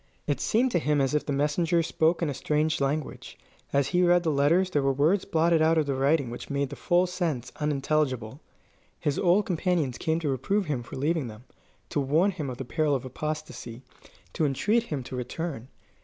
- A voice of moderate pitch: Yes, medium, 150 Hz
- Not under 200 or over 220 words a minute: Yes, fast, 205 wpm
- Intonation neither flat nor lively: Yes, average, 3.8 semitones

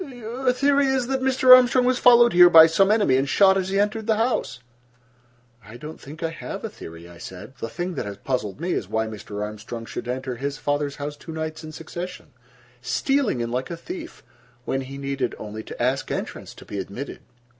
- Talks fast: Yes, fast, 210 wpm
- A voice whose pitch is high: No, medium, 160 Hz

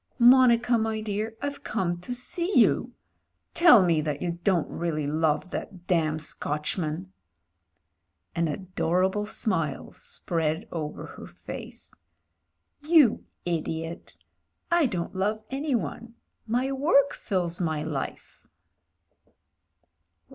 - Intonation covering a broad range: Yes, wide, 6.4 semitones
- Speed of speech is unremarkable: No, slow, 105 wpm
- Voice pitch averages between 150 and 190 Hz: Yes, medium, 185 Hz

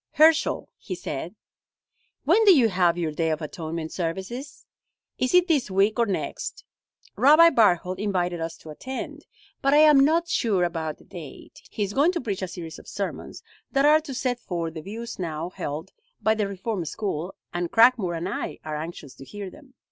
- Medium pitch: No, high, 195 Hz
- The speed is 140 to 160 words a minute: No, average, 190 wpm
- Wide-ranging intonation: Yes, wide, 7.5 semitones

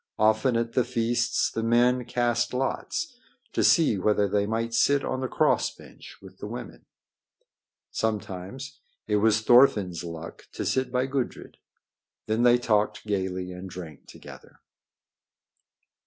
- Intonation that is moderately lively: Yes, average, 3.4 semitones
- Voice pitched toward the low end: Yes, low, 115 Hz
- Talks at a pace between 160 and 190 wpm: No, average, 140 wpm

